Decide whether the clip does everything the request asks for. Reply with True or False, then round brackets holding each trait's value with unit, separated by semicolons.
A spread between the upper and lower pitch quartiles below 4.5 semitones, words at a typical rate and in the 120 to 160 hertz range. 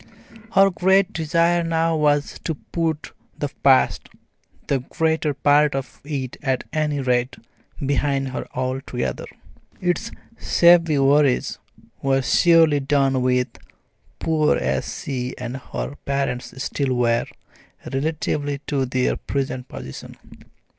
False (3.5 semitones; 115 wpm; 140 Hz)